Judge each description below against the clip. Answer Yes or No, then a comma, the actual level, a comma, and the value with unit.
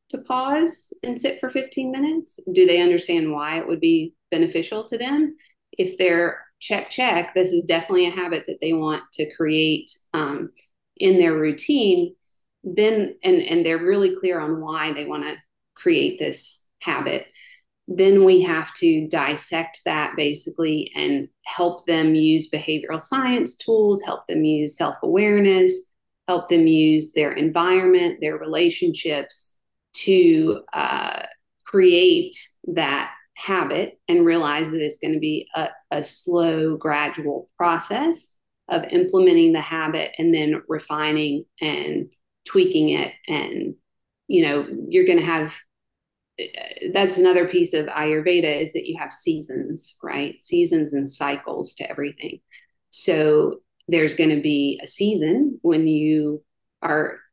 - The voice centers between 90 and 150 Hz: No, medium, 180 Hz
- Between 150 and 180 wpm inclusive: No, average, 140 wpm